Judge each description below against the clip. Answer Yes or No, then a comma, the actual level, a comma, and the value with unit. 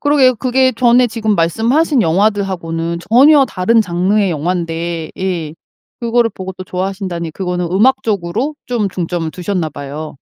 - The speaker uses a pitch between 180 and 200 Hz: Yes, high, 190 Hz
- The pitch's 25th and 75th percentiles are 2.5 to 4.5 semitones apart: No, wide, 5.4 semitones